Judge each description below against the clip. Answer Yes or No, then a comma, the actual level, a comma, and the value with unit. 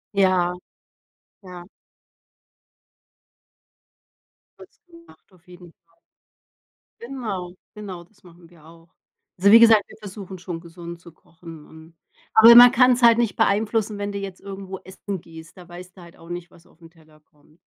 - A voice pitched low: No, medium, 180 Hz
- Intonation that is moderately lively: Yes, average, 3.5 semitones